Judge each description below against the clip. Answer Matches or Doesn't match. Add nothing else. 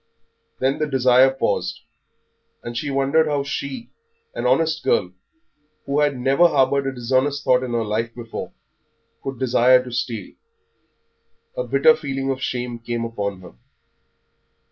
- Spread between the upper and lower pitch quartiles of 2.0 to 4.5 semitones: Matches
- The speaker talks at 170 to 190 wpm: Doesn't match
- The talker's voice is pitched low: Matches